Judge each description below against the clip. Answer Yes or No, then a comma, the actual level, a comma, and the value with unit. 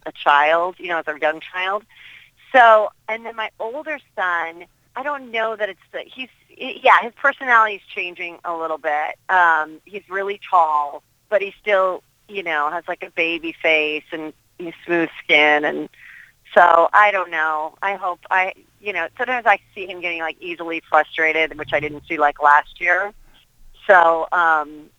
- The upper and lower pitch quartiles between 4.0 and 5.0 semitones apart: Yes, average, 4.5 semitones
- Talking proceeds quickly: No, average, 175 wpm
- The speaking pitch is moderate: Yes, medium, 170 Hz